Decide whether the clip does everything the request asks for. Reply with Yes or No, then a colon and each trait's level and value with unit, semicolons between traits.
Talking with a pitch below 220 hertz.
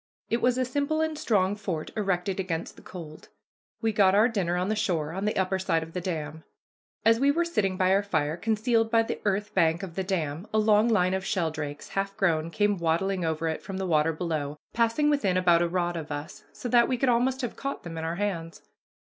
Yes: high, 190 Hz